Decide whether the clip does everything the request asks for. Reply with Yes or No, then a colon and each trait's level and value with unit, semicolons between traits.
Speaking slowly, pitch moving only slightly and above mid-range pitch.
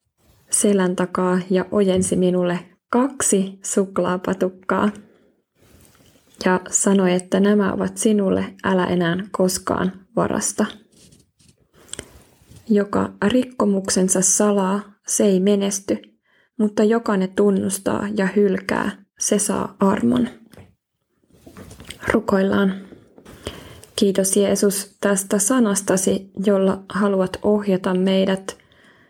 Yes: slow, 85 wpm; narrow, 1.7 semitones; high, 195 Hz